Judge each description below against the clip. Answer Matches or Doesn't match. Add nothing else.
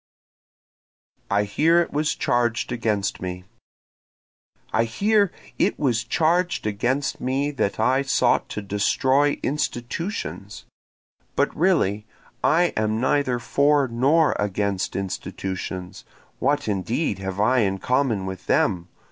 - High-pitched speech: Doesn't match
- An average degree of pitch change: Doesn't match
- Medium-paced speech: Doesn't match